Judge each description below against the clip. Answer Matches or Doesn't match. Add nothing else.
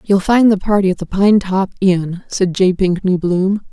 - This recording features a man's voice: Doesn't match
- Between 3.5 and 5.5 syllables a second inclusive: Matches